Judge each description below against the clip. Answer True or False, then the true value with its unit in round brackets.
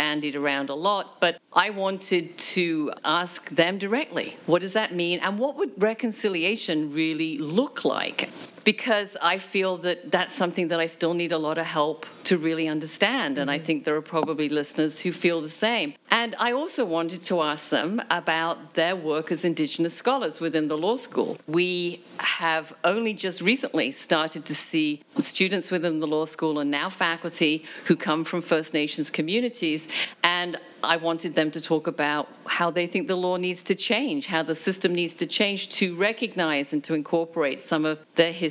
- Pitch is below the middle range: False (175 Hz)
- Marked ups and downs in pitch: False (3.6 semitones)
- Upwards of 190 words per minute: False (185 wpm)